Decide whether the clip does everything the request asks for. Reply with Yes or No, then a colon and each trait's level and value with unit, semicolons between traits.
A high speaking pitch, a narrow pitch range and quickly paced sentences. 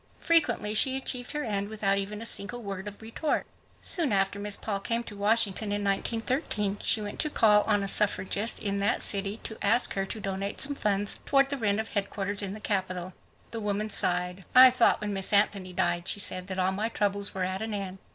Yes: high, 205 Hz; narrow, 2.2 semitones; fast, 215 wpm